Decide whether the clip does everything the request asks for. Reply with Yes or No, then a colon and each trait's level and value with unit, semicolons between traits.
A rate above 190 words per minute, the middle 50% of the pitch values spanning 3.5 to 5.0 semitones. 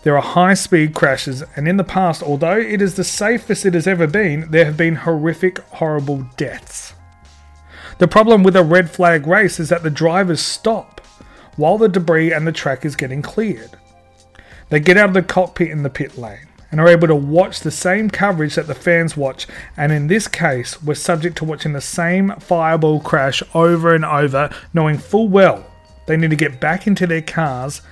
Yes: average, 200 wpm; average, 4.0 semitones